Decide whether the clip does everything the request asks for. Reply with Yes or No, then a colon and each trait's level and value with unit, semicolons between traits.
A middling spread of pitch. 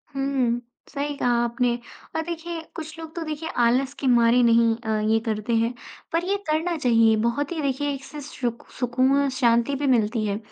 Yes: average, 4.0 semitones